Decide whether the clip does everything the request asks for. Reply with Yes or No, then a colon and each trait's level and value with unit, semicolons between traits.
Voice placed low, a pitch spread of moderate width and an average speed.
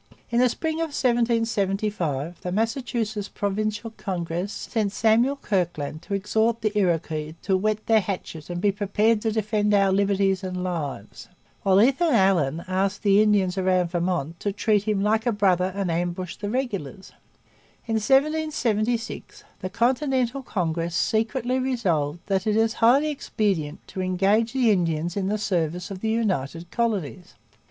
No: high, 200 Hz; average, 3.8 semitones; average, 150 wpm